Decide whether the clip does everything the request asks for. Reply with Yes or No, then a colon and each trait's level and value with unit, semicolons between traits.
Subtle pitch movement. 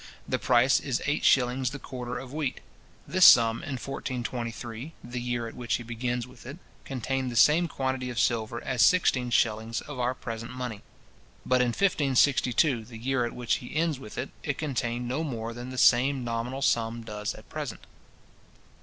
Yes: narrow, 2.3 semitones